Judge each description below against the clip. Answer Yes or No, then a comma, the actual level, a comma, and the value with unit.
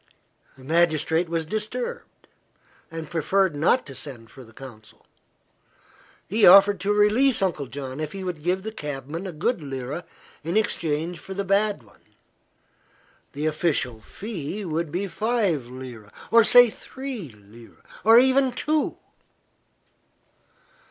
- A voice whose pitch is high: No, medium, 170 Hz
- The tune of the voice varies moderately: No, wide, 6.7 semitones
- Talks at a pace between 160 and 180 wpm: No, slow, 135 wpm